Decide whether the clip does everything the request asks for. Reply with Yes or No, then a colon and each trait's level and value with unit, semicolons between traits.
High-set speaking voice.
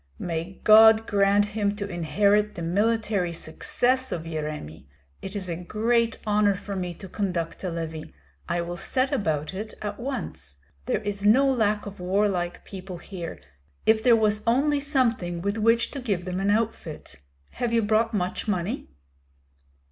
Yes: high, 205 Hz